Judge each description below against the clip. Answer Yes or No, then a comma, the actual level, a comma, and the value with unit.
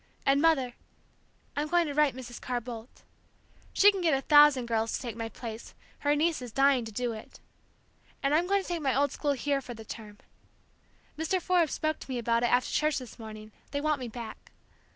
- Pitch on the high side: Yes, very high, 270 Hz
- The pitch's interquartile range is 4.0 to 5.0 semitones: Yes, average, 4.4 semitones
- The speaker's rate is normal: No, fast, 215 wpm